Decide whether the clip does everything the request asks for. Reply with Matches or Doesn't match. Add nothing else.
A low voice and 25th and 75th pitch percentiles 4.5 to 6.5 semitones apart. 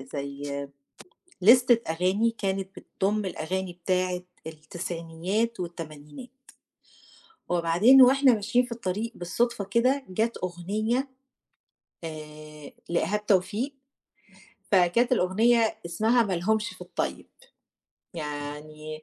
Doesn't match